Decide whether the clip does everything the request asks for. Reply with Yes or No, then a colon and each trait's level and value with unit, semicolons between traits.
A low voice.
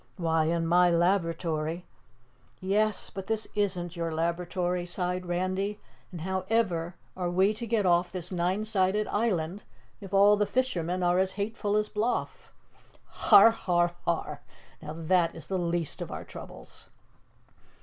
No: medium, 180 Hz